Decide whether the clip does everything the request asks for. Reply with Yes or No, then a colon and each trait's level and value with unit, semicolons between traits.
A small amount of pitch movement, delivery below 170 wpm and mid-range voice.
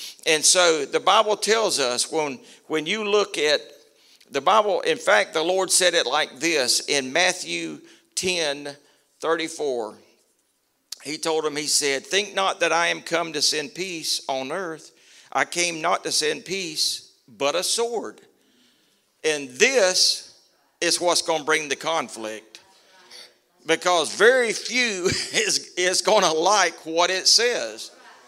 No: average, 4.8 semitones; average, 150 wpm; medium, 170 Hz